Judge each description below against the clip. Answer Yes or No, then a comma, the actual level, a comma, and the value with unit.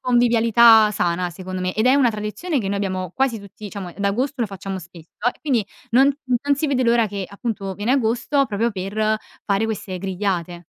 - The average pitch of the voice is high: Yes, high, 210 Hz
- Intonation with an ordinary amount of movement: Yes, average, 3.9 semitones